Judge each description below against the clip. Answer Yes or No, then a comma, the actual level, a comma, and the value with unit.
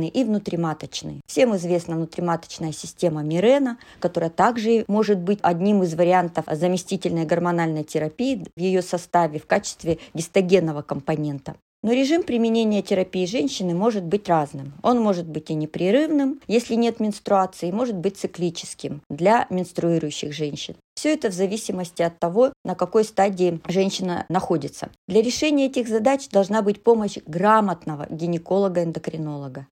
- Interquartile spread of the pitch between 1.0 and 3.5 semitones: No, average, 4.8 semitones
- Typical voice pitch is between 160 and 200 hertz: Yes, medium, 185 Hz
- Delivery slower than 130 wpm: No, average, 135 wpm